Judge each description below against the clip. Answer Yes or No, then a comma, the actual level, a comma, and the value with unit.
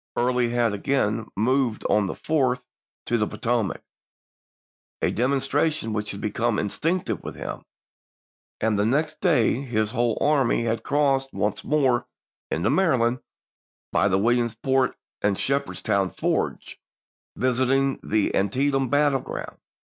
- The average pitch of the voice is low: Yes, low, 120 Hz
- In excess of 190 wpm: No, average, 140 wpm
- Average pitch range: Yes, average, 3.9 semitones